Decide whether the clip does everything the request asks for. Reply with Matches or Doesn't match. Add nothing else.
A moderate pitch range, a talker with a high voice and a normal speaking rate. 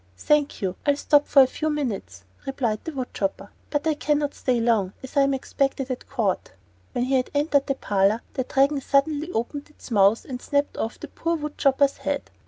Doesn't match